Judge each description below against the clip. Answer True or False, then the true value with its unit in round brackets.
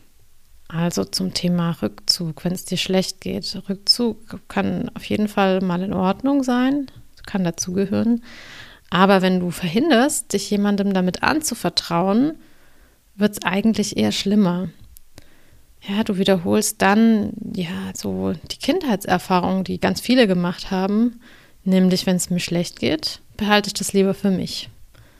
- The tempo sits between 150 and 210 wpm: False (140 wpm)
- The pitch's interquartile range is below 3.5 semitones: True (2.7 semitones)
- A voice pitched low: False (195 Hz)